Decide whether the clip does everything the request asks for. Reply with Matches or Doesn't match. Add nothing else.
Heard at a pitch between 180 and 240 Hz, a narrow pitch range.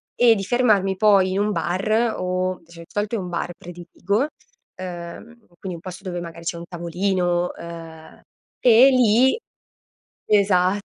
Doesn't match